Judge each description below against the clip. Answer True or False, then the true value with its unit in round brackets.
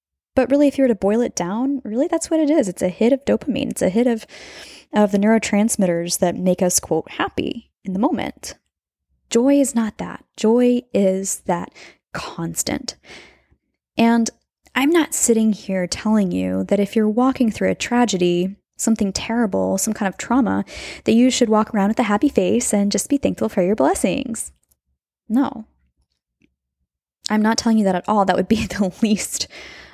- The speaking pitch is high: True (215 Hz)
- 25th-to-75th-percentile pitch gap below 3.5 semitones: False (5.1 semitones)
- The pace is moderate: True (180 wpm)